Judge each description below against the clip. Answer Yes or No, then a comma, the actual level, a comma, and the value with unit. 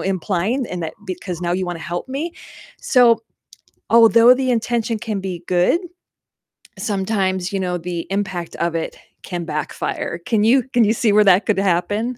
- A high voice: Yes, high, 195 Hz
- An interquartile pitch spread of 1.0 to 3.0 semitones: No, average, 4.4 semitones